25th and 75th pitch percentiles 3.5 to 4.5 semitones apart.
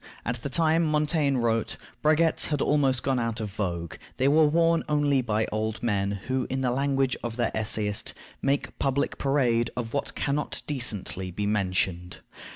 No: average, 4.9 semitones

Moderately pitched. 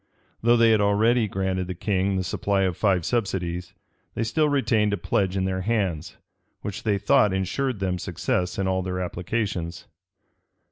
No: very low, 95 Hz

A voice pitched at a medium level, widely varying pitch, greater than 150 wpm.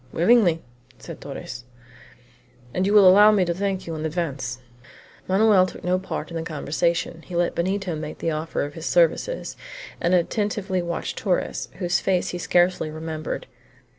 No: medium, 175 Hz; average, 2.8 semitones; average, 165 wpm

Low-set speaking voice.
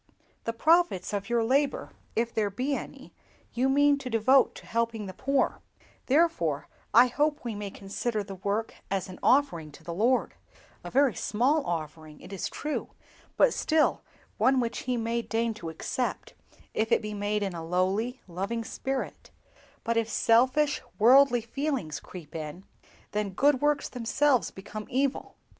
No: high, 230 Hz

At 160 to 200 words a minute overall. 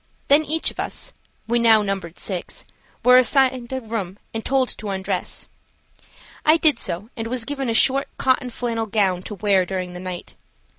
Yes: average, 165 wpm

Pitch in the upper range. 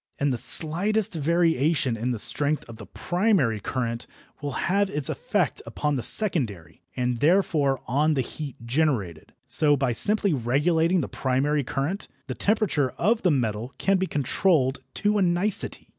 No: medium, 145 Hz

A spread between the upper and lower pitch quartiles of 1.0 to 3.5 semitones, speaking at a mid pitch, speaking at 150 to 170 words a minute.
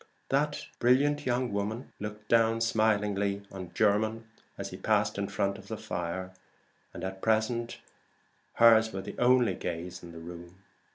No: average, 3.2 semitones; low, 105 Hz; average, 160 wpm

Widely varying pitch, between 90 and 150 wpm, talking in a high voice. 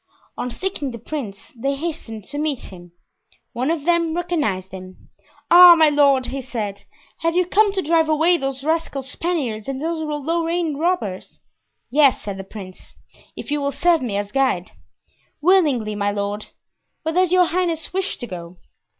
No: wide, 7.4 semitones; average, 165 wpm; very high, 290 Hz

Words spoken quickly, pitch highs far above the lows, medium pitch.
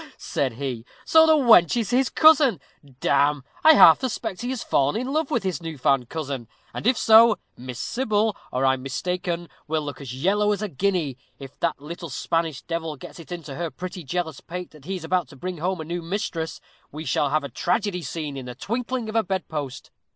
Yes: fast, 215 wpm; wide, 6.6 semitones; medium, 170 Hz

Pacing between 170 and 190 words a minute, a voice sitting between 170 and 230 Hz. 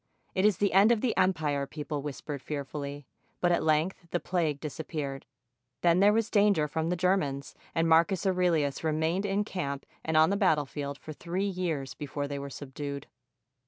No: average, 180 wpm; medium, 160 Hz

